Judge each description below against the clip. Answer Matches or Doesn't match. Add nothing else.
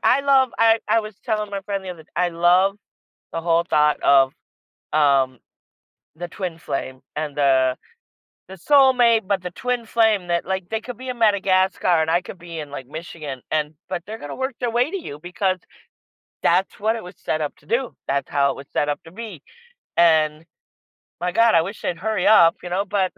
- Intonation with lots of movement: Matches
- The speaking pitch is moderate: Matches